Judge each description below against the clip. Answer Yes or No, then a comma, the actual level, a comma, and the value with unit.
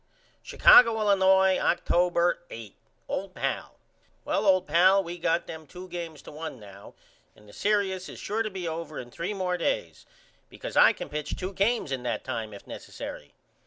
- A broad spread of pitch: No, average, 4.0 semitones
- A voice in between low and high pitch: Yes, medium, 175 Hz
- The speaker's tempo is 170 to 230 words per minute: Yes, average, 175 wpm